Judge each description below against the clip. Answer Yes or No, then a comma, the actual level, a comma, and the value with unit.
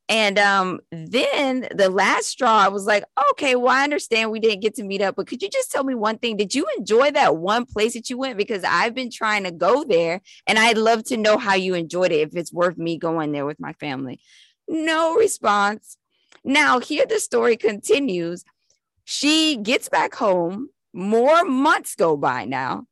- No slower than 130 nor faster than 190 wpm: No, average, 200 wpm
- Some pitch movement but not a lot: No, wide, 6.4 semitones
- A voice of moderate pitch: No, high, 220 Hz